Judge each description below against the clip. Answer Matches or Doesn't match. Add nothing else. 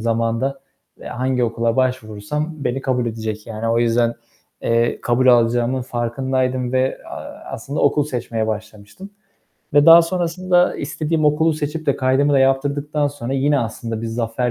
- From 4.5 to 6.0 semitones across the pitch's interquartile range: Doesn't match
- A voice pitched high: Doesn't match